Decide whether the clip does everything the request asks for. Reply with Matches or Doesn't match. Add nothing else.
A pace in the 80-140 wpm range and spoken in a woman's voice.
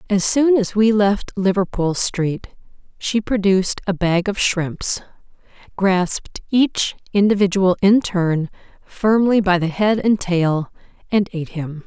Matches